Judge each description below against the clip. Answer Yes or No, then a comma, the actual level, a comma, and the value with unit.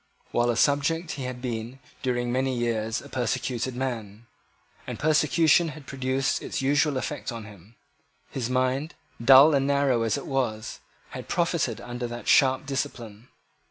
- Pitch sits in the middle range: No, low, 130 Hz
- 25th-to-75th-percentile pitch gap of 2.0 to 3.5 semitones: Yes, average, 2.9 semitones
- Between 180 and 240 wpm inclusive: No, average, 155 wpm